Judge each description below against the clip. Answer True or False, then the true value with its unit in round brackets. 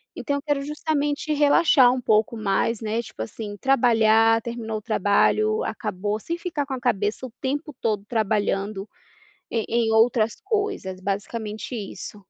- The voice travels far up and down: False (4.4 semitones)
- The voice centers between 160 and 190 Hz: False (225 Hz)